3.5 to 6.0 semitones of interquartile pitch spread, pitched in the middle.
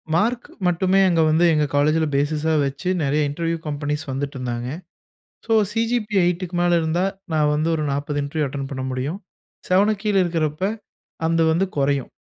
Yes: average, 3.9 semitones; medium, 160 Hz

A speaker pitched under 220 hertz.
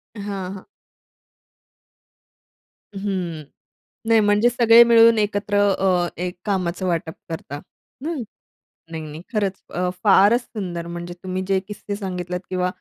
Yes: high, 190 Hz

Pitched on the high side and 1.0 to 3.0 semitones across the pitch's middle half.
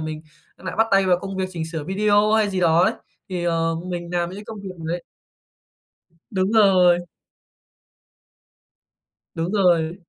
No: medium, 180 Hz; narrow, 2.5 semitones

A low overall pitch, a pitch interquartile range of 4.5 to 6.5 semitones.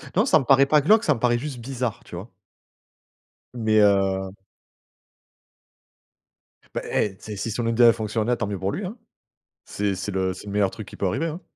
Yes: low, 110 Hz; average, 4.9 semitones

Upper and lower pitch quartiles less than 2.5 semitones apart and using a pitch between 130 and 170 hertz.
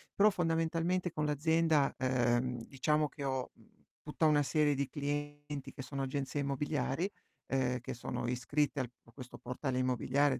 No: average, 2.8 semitones; medium, 140 Hz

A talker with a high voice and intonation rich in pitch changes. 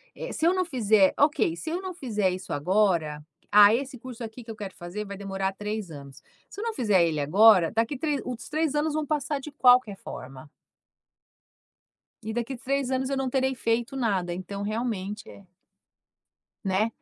Yes: high, 220 Hz; wide, 5.7 semitones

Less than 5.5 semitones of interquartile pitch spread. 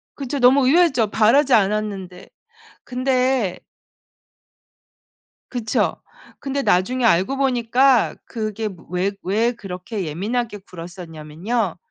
Yes: average, 5.1 semitones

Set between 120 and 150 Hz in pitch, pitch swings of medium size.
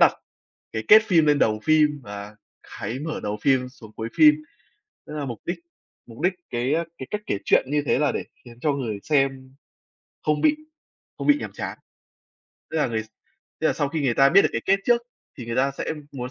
Yes: low, 135 Hz; average, 4.5 semitones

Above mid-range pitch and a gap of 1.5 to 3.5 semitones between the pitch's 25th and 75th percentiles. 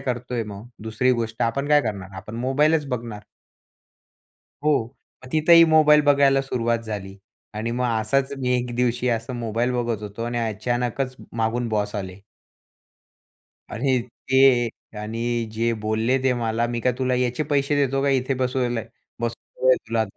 No: low, 120 Hz; average, 2.8 semitones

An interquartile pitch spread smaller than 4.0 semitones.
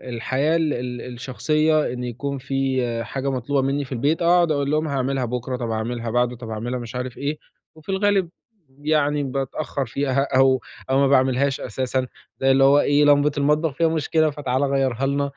Yes: average, 2.7 semitones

